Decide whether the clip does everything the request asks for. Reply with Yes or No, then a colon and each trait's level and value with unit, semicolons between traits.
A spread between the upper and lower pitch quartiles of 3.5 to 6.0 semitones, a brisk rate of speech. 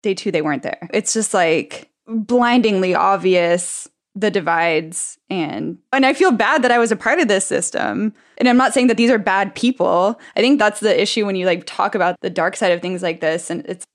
Yes: average, 5.0 semitones; fast, 230 wpm